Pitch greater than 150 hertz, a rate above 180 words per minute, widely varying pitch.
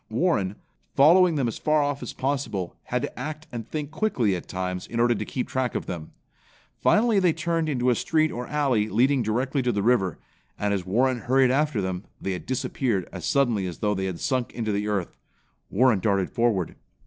No: low, 120 Hz; average, 200 wpm; wide, 5.8 semitones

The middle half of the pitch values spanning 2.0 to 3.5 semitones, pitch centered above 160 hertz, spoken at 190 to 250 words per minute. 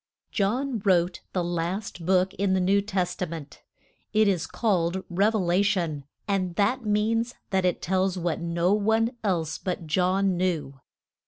No: average, 2.9 semitones; medium, 185 Hz; average, 165 wpm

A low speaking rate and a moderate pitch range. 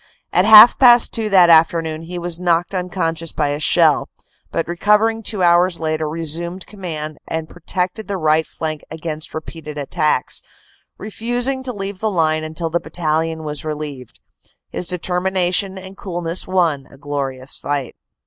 No: average, 155 wpm; average, 3.2 semitones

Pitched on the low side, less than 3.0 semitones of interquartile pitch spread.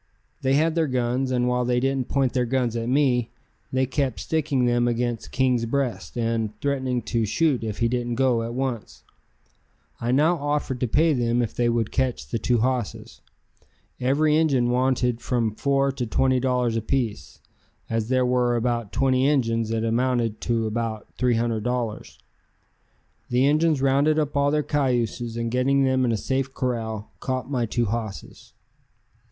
Yes: low, 125 Hz; narrow, 2.4 semitones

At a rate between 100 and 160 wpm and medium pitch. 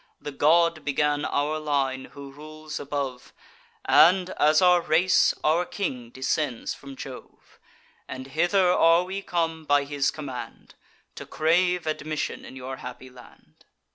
Yes: average, 140 wpm; medium, 150 Hz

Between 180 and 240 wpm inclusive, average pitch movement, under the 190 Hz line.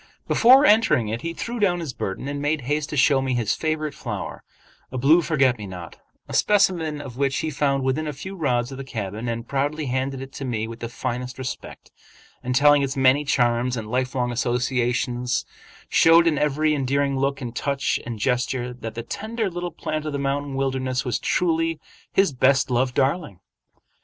Yes: average, 190 wpm; average, 3.6 semitones; low, 135 Hz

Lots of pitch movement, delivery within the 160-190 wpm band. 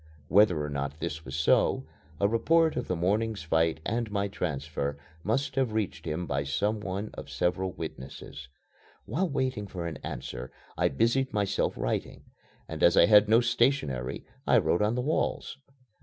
Yes: wide, 6.3 semitones; average, 170 wpm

